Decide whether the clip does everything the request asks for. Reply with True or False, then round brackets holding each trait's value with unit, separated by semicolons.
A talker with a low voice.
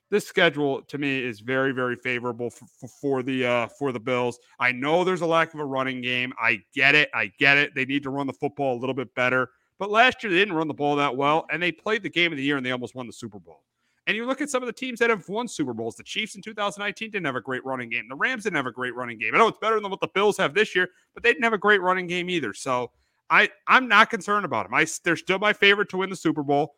False (145 Hz)